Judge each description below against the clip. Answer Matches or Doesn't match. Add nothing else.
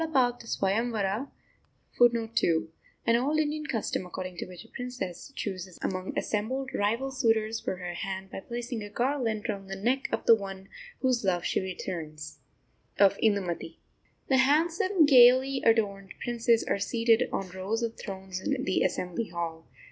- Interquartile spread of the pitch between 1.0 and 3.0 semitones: Doesn't match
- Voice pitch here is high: Matches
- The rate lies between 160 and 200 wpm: Doesn't match